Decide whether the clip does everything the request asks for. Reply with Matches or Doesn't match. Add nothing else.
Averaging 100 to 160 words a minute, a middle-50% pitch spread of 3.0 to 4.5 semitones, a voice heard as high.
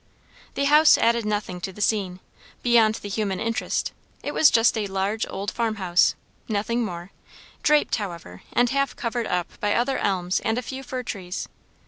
Doesn't match